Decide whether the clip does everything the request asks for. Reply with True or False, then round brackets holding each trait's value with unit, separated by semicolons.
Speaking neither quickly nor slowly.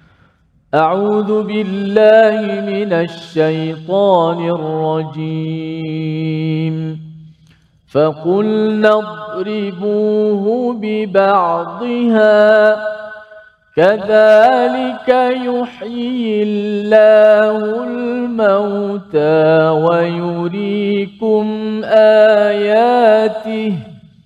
False (35 wpm)